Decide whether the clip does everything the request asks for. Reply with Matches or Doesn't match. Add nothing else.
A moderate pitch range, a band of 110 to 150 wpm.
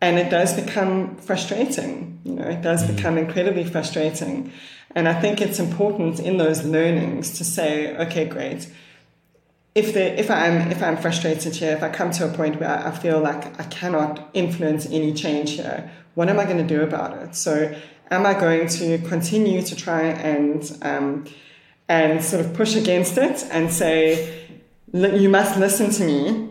Doesn't match